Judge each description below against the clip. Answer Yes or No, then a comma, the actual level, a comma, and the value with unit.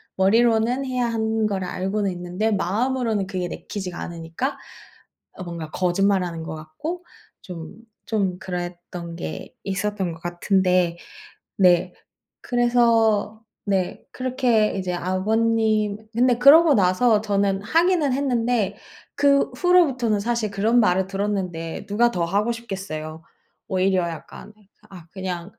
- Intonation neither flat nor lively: Yes, average, 4.5 semitones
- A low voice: No, high, 200 Hz